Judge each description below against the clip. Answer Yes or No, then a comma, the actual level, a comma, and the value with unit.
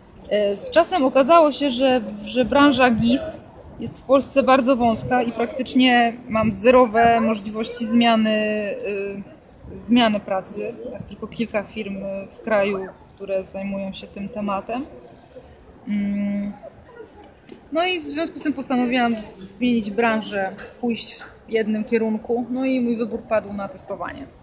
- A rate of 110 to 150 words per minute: Yes, average, 130 wpm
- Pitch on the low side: No, high, 230 Hz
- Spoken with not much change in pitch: No, average, 3.7 semitones